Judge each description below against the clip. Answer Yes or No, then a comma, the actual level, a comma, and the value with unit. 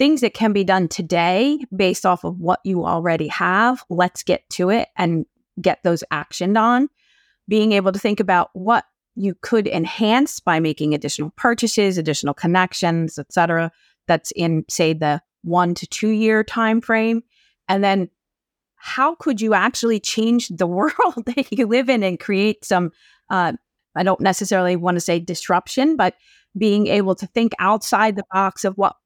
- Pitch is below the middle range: No, high, 195 Hz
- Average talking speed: Yes, average, 170 wpm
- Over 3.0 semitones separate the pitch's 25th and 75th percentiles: Yes, average, 4.2 semitones